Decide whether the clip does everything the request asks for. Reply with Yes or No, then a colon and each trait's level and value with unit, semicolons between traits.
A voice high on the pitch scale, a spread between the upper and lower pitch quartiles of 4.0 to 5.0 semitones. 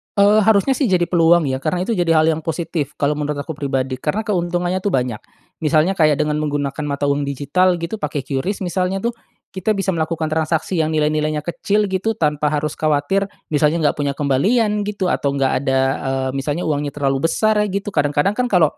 No: medium, 155 Hz; average, 4.5 semitones